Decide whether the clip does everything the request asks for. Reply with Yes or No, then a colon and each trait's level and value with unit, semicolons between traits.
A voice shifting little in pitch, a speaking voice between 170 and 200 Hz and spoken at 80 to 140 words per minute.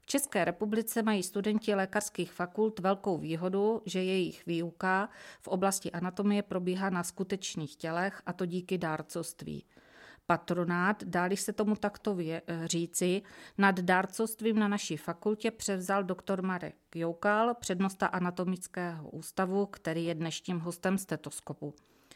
No: average, 3.0 semitones; medium, 185 Hz; average, 125 wpm